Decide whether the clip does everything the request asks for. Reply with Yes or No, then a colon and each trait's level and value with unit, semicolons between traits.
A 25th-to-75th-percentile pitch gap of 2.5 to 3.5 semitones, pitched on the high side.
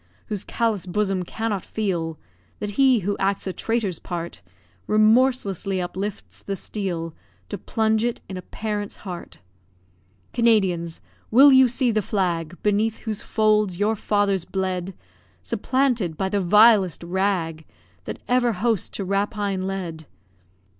Yes: average, 3.1 semitones; high, 200 Hz